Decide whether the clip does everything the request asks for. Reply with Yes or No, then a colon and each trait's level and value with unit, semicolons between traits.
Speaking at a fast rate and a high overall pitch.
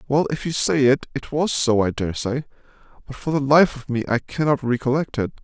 No: fast, 220 wpm; low, 135 Hz